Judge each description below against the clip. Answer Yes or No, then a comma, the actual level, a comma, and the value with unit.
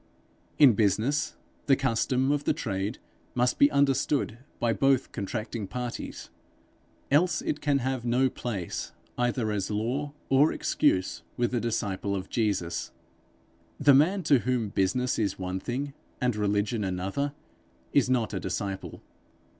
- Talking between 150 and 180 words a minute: No, average, 140 wpm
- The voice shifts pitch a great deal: No, average, 5.0 semitones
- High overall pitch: No, low, 120 Hz